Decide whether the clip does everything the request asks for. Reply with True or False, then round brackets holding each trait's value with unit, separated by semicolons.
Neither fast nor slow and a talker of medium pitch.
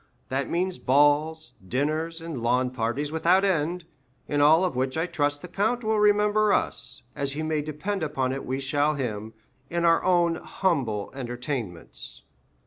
True (160 wpm; 150 Hz)